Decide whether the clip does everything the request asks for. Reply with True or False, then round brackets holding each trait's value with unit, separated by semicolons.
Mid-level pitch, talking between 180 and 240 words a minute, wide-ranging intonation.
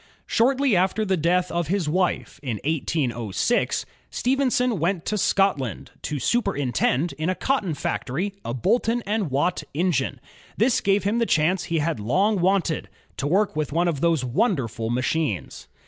False (175 Hz; 155 wpm; 5.9 semitones)